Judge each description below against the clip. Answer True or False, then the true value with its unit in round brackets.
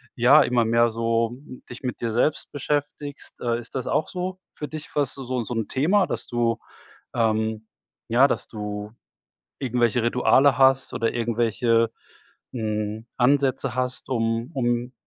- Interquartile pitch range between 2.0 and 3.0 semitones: True (2.7 semitones)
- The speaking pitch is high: False (120 Hz)